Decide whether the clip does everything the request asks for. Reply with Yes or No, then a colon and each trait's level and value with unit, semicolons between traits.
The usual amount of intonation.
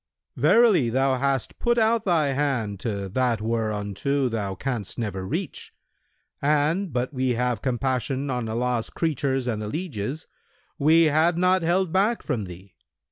No: wide, 5.9 semitones